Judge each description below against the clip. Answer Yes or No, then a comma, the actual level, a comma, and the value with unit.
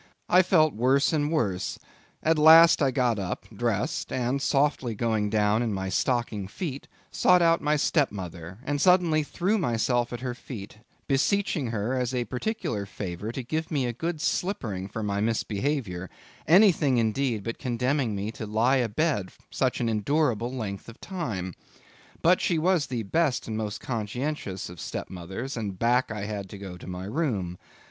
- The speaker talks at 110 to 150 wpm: No, average, 165 wpm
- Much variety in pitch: Yes, wide, 6.2 semitones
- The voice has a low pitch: Yes, low, 120 Hz